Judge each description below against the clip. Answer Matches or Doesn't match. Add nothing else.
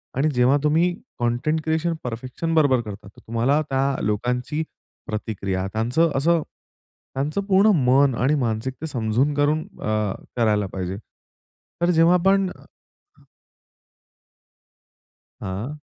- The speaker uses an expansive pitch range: Matches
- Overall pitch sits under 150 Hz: Matches